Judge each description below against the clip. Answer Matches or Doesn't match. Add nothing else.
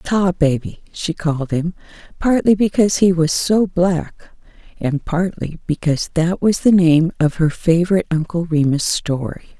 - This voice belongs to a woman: Matches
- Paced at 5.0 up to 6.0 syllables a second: Doesn't match